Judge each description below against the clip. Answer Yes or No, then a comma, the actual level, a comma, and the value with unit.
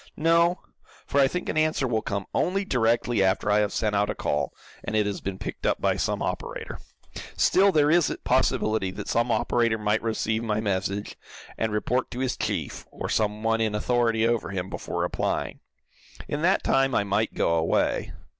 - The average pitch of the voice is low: Yes, low, 110 Hz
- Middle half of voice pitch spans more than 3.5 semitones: Yes, average, 4.2 semitones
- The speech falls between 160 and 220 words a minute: Yes, average, 190 wpm